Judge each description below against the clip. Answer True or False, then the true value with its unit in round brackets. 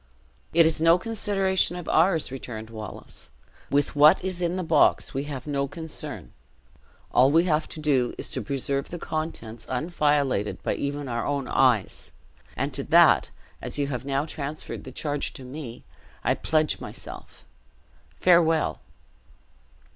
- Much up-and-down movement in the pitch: False (3.5 semitones)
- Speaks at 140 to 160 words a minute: True (150 wpm)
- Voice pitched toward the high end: False (145 Hz)